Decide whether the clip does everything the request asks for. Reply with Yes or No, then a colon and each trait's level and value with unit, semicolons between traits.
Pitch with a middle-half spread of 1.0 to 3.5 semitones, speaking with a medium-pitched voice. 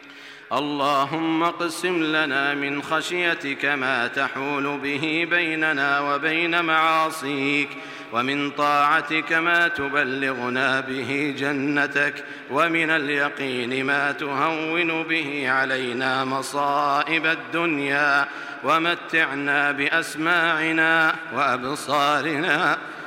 Yes: narrow, 2.4 semitones; medium, 145 Hz